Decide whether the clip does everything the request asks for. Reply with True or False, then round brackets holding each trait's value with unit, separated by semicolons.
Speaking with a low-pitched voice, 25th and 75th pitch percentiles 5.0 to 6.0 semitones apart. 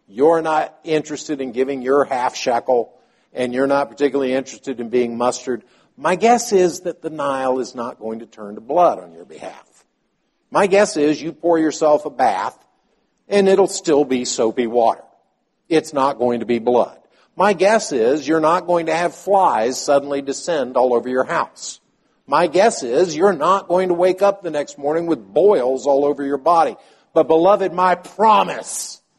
False (145 Hz; 5.4 semitones)